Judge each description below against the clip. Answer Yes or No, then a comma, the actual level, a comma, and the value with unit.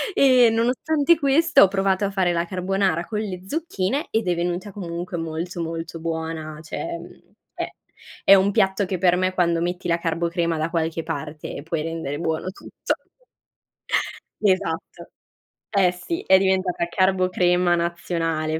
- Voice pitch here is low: No, medium, 180 Hz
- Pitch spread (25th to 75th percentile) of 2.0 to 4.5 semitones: Yes, average, 2.7 semitones